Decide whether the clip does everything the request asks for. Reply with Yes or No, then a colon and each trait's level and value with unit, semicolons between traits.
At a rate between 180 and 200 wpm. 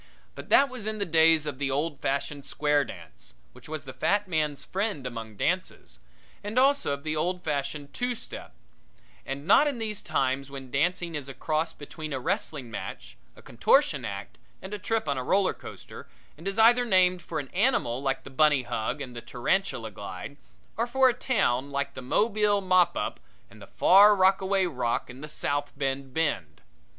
Yes: average, 190 wpm